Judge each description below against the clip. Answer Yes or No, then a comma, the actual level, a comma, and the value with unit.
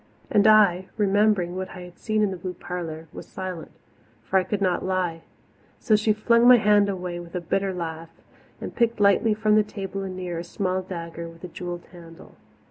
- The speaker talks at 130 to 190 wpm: No, average, 200 wpm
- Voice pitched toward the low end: No, medium, 185 Hz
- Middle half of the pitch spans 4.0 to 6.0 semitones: No, average, 3.0 semitones